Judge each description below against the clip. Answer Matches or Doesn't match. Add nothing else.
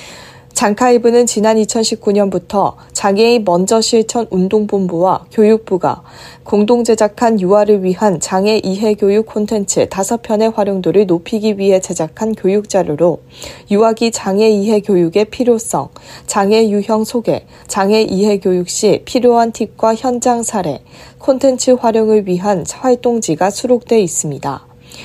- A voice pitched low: Doesn't match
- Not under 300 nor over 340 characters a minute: Doesn't match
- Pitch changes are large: Doesn't match